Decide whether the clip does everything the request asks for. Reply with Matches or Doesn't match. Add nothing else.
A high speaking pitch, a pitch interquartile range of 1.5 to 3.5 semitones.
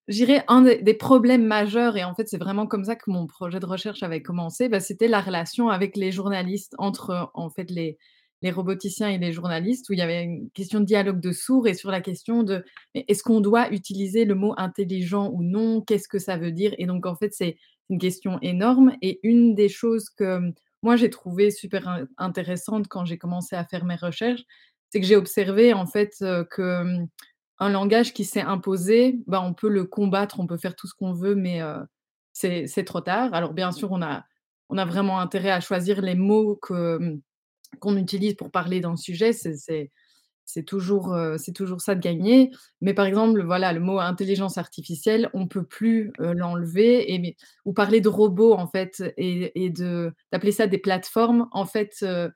Matches